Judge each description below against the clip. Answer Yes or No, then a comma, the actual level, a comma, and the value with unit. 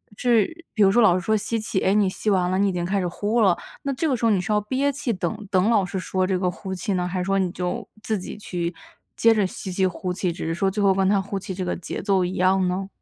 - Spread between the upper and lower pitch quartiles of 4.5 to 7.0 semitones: No, average, 2.7 semitones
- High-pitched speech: Yes, high, 195 Hz